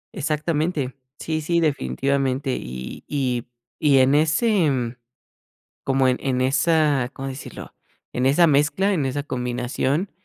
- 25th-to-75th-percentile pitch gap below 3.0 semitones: No, average, 3.3 semitones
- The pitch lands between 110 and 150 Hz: Yes, medium, 140 Hz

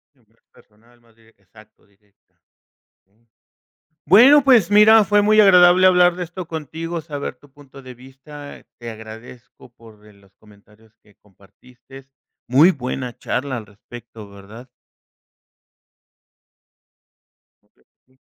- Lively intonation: Yes, wide, 7.2 semitones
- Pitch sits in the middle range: No, low, 125 Hz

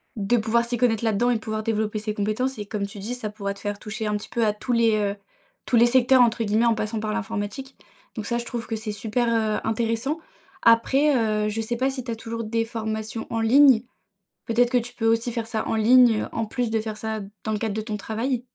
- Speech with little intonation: Yes, narrow, 1.9 semitones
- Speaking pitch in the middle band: No, high, 225 Hz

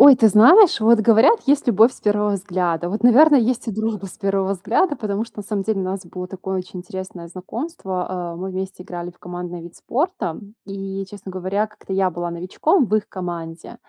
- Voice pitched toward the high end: Yes, high, 195 Hz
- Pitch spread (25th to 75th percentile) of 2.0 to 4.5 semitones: Yes, average, 3.4 semitones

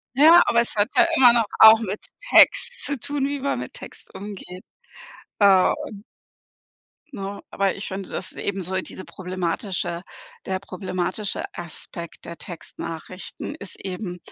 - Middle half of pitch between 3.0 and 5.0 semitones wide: Yes, average, 3.7 semitones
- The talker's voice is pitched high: Yes, high, 195 Hz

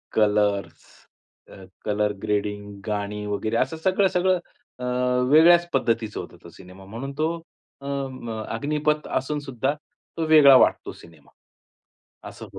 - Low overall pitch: Yes, low, 115 Hz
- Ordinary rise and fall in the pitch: No, wide, 6.5 semitones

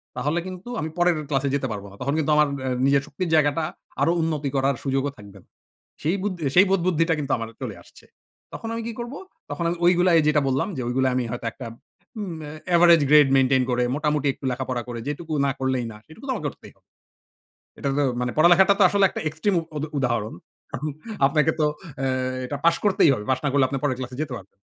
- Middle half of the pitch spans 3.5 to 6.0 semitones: Yes, average, 4.3 semitones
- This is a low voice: No, medium, 145 Hz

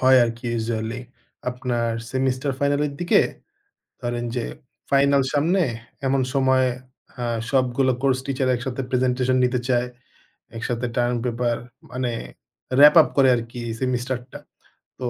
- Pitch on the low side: Yes, low, 130 Hz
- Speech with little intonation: Yes, narrow, 1.8 semitones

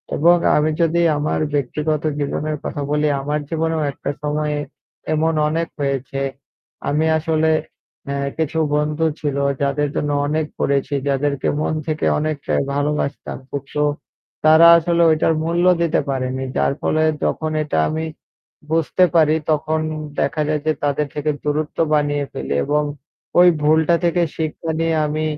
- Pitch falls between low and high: Yes, medium, 150 Hz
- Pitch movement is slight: Yes, narrow, 1.6 semitones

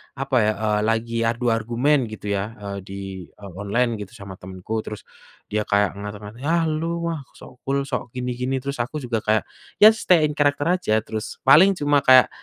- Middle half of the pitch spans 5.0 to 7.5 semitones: Yes, average, 5.3 semitones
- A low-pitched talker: Yes, low, 120 Hz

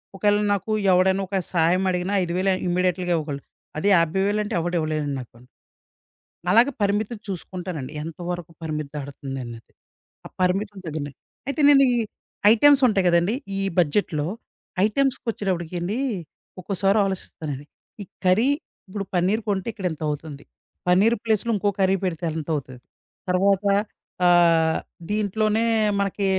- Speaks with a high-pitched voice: No, medium, 180 Hz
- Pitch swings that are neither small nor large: Yes, average, 4.1 semitones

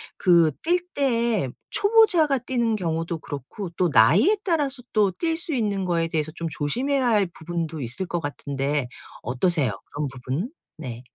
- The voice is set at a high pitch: No, medium, 175 Hz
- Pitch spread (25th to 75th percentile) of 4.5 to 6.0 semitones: No, wide, 9.0 semitones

